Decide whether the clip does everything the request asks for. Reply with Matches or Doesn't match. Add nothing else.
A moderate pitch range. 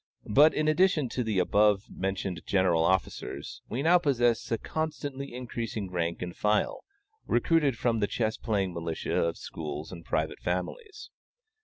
Doesn't match